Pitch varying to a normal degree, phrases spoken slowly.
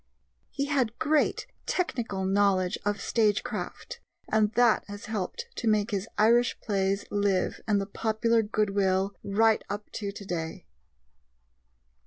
No: narrow, 2.3 semitones; slow, 125 wpm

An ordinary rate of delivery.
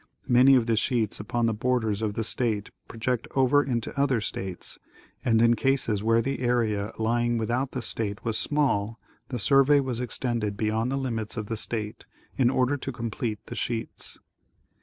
Yes: average, 175 wpm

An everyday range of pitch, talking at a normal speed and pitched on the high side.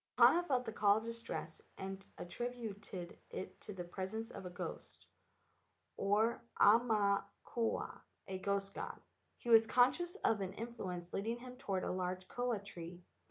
Yes: average, 3.6 semitones; average, 155 wpm; high, 205 Hz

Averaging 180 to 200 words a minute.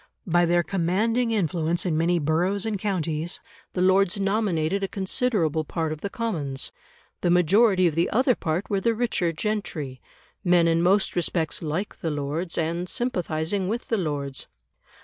No: average, 160 wpm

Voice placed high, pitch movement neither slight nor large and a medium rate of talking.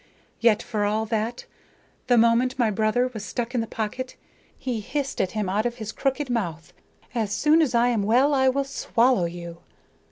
Yes: high, 230 Hz; average, 3.2 semitones; average, 190 wpm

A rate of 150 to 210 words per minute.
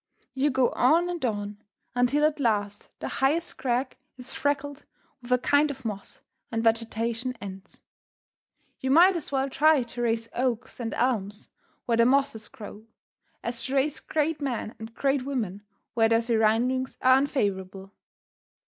Yes: average, 155 wpm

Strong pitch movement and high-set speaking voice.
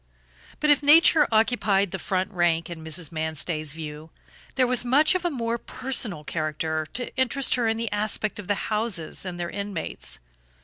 Yes: wide, 7.0 semitones; high, 200 Hz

